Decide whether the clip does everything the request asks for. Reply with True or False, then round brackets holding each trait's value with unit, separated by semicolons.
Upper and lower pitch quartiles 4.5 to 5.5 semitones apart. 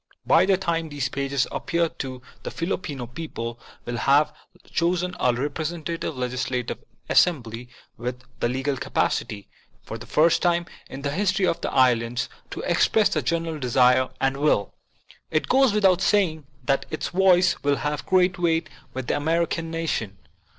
True (5.0 semitones)